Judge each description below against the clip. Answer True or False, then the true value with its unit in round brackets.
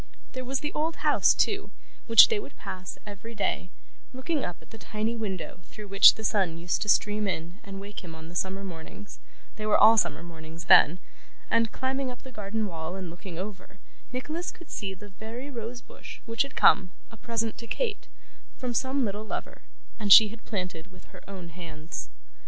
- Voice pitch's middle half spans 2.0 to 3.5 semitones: False (4.2 semitones)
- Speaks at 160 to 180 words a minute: False (200 wpm)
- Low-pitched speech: False (210 Hz)